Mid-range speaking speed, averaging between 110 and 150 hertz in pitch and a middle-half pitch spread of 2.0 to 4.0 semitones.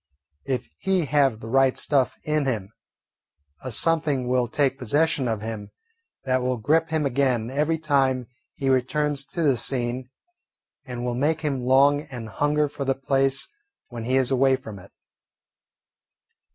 Yes: average, 155 wpm; low, 135 Hz; average, 2.9 semitones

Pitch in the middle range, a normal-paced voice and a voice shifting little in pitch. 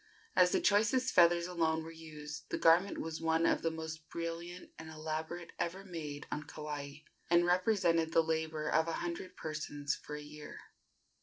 Yes: medium, 160 Hz; average, 170 wpm; narrow, 1.9 semitones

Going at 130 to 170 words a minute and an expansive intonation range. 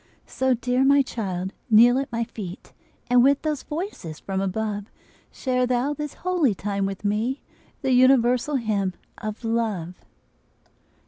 No: average, 140 wpm; average, 4.5 semitones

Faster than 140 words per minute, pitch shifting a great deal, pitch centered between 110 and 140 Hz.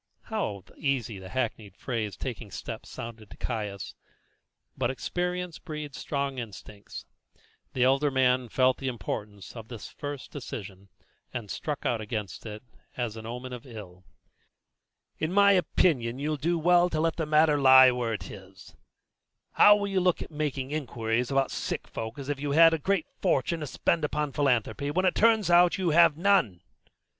Yes: average, 170 wpm; wide, 5.8 semitones; low, 135 Hz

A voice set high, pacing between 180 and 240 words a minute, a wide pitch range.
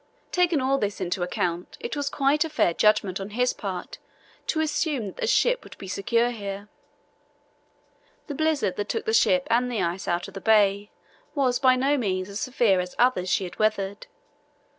Yes: high, 220 Hz; average, 190 wpm; wide, 5.9 semitones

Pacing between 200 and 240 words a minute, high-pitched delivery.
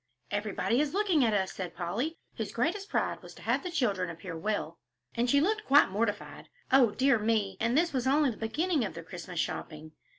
Yes: fast, 205 wpm; high, 230 Hz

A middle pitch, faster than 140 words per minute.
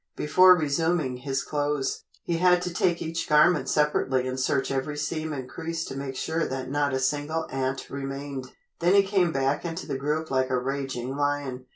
Yes: medium, 145 Hz; average, 190 wpm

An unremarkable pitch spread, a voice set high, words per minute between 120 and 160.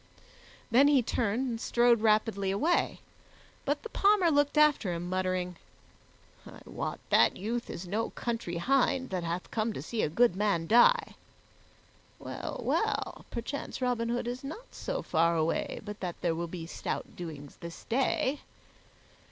No: wide, 6.5 semitones; high, 225 Hz; average, 155 wpm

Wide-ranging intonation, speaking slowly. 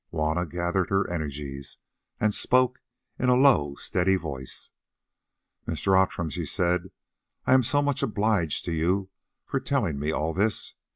No: wide, 6.0 semitones; average, 150 wpm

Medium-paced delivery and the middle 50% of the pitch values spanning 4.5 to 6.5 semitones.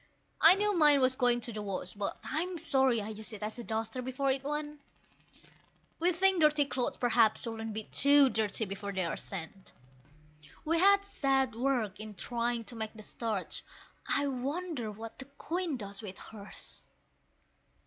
Yes: average, 170 wpm; average, 5.0 semitones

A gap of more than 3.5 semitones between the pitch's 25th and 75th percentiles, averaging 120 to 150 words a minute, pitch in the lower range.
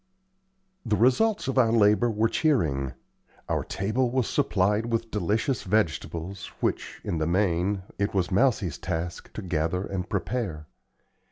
Yes: average, 4.8 semitones; average, 140 wpm; low, 105 Hz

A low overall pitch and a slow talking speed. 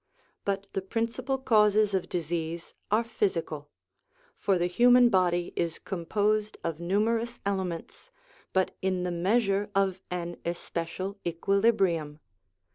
No: high, 190 Hz; slow, 120 wpm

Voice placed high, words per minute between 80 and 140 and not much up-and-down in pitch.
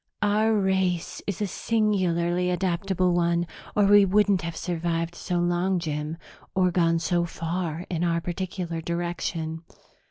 No: medium, 175 Hz; slow, 135 wpm; narrow, 2.1 semitones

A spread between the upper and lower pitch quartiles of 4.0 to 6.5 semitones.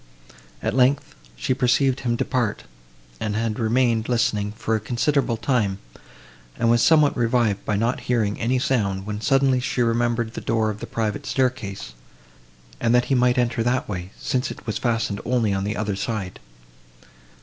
No: average, 2.8 semitones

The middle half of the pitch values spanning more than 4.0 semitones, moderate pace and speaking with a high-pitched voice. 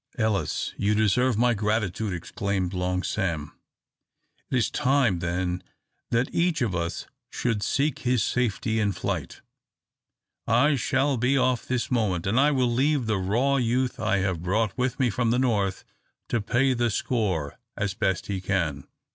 No: average, 4.7 semitones; average, 160 wpm; low, 110 Hz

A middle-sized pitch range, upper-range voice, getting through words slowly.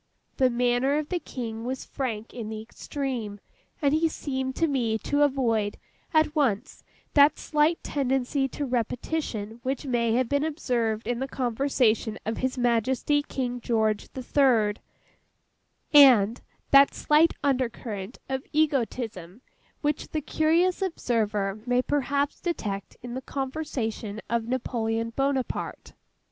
Yes: average, 4.0 semitones; very high, 255 Hz; slow, 130 wpm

